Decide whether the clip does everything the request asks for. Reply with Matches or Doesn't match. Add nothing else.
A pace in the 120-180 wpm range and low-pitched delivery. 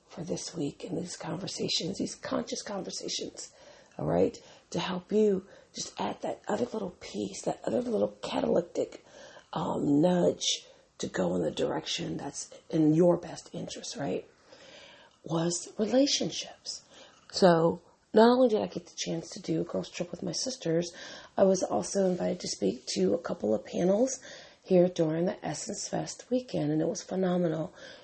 Doesn't match